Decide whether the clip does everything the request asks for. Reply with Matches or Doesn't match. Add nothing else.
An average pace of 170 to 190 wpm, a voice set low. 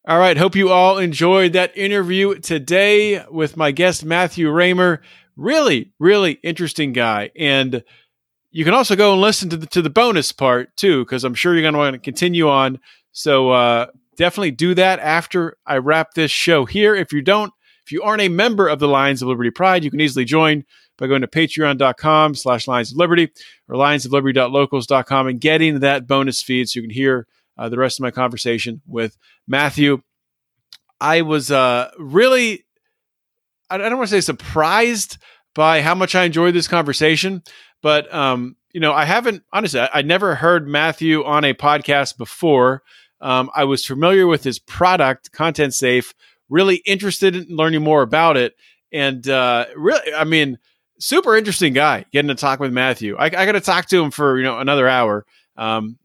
Doesn't match